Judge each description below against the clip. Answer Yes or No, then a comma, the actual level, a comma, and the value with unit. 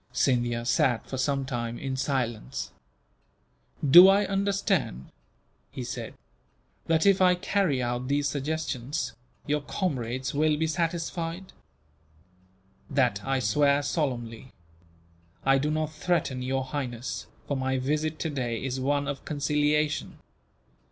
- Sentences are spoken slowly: Yes, slow, 120 wpm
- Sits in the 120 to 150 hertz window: Yes, medium, 140 Hz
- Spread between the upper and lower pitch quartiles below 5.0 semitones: Yes, average, 3.6 semitones